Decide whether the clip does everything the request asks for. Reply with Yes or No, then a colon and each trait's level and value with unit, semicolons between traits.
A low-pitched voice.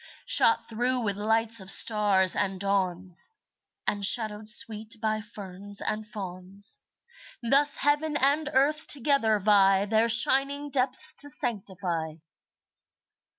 No: high, 215 Hz